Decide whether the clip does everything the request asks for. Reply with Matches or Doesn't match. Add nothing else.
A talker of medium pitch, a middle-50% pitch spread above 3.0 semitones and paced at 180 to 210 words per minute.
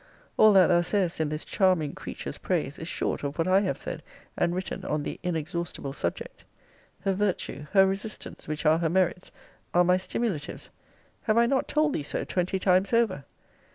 Matches